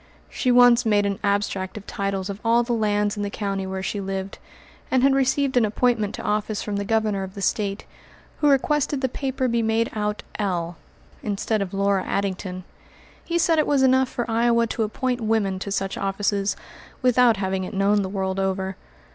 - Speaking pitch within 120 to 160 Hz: No, high, 210 Hz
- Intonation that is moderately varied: Yes, average, 3.5 semitones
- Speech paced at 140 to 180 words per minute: No, average, 195 wpm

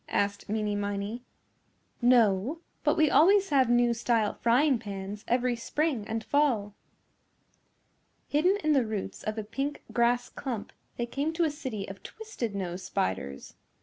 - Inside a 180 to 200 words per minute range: No, average, 150 wpm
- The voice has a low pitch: No, high, 235 Hz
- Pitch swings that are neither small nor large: No, wide, 5.7 semitones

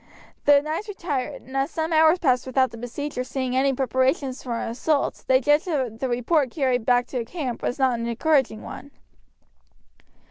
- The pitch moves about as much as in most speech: Yes, average, 3.1 semitones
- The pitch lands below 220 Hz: No, very high, 265 Hz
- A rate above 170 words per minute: Yes, average, 180 wpm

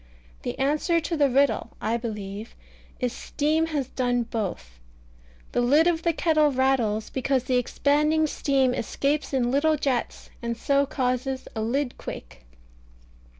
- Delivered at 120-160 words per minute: Yes, average, 145 wpm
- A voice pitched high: Yes, very high, 265 Hz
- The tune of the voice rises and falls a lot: No, average, 3.6 semitones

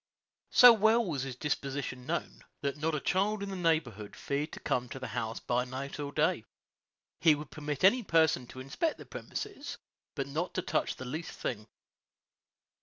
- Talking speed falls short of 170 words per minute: No, average, 180 wpm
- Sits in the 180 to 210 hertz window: No, medium, 145 Hz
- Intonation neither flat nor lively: No, wide, 5.8 semitones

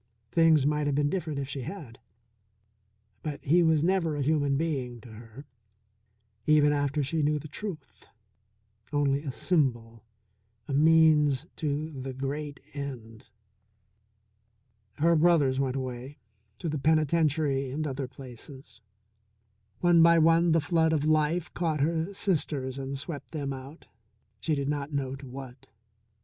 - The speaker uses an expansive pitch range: No, average, 2.9 semitones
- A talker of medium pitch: Yes, medium, 145 Hz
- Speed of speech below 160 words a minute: Yes, average, 140 wpm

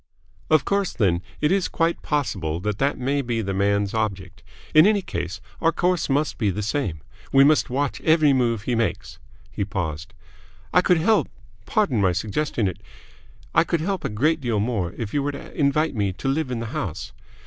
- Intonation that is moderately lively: No, wide, 7.3 semitones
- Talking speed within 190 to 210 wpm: Yes, average, 195 wpm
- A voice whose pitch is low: Yes, low, 125 Hz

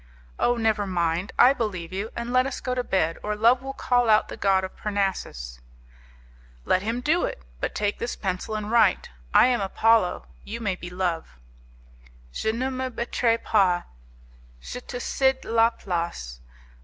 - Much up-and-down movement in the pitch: No, average, 4.7 semitones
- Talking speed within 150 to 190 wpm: Yes, average, 170 wpm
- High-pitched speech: Yes, high, 215 Hz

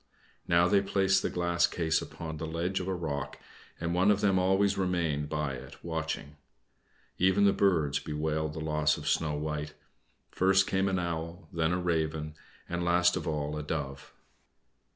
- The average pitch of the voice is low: Yes, very low, 85 Hz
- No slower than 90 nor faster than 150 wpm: No, average, 175 wpm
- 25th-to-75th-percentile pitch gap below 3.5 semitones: Yes, average, 3.1 semitones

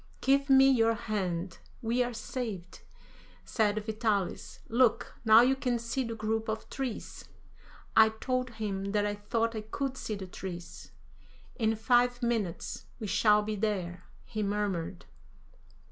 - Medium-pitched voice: No, high, 220 Hz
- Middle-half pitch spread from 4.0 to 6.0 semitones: No, average, 2.8 semitones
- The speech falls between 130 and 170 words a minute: Yes, average, 145 wpm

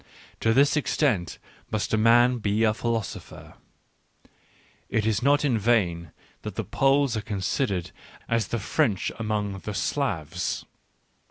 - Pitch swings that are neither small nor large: Yes, average, 3.6 semitones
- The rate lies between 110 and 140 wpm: Yes, slow, 135 wpm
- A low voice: Yes, low, 110 Hz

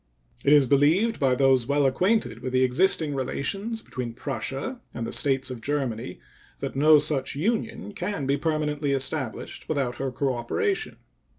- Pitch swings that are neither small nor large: Yes, average, 3.4 semitones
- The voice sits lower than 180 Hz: Yes, medium, 140 Hz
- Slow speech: No, average, 155 wpm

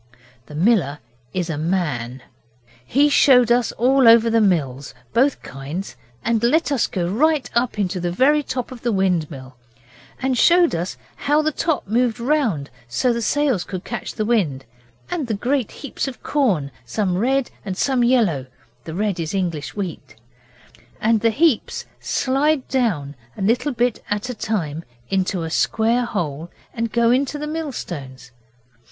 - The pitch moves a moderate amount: No, wide, 7.0 semitones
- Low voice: No, high, 220 Hz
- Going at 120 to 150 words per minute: No, average, 170 wpm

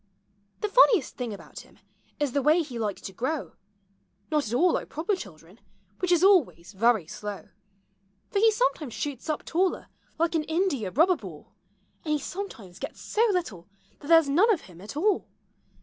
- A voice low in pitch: No, very high, 295 Hz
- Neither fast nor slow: Yes, average, 185 wpm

